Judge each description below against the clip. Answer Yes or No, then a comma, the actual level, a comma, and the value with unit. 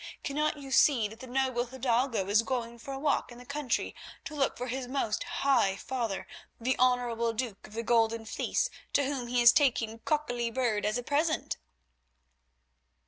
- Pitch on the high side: Yes, high, 245 Hz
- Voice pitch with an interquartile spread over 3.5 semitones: No, average, 2.7 semitones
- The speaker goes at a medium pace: Yes, average, 185 wpm